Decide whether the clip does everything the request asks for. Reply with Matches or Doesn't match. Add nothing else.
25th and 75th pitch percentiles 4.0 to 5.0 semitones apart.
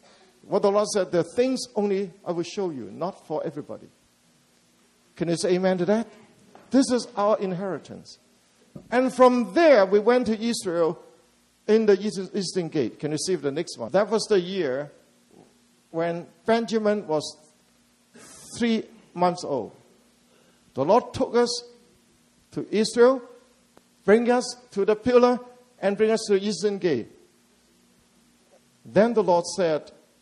Matches